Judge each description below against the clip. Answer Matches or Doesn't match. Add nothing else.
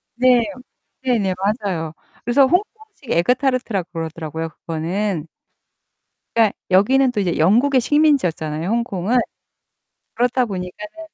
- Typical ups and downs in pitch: Doesn't match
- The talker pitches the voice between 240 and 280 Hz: Doesn't match